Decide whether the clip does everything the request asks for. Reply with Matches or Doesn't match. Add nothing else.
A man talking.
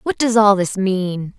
Doesn't match